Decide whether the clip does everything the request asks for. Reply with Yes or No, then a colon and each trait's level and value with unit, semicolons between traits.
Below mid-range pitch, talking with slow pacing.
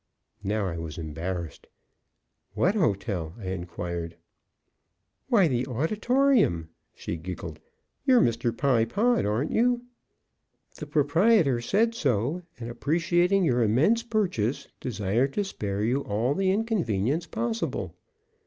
Yes: low, 130 Hz; slow, 115 wpm